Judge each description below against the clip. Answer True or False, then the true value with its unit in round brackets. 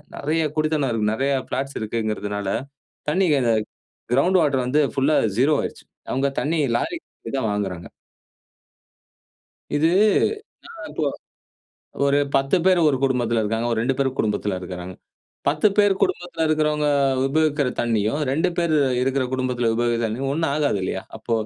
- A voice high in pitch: False (135 Hz)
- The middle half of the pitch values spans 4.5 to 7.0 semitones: True (5.0 semitones)